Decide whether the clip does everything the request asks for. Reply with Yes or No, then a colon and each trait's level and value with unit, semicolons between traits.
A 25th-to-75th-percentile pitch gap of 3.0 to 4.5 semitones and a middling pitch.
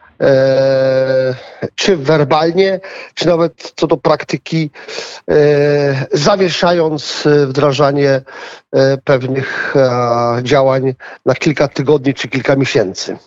Yes: average, 3.5 semitones; medium, 145 Hz